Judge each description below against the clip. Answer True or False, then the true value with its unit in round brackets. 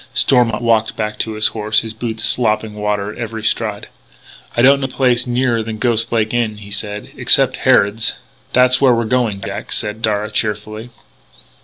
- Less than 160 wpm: False (180 wpm)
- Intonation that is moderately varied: False (2.1 semitones)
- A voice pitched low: True (110 Hz)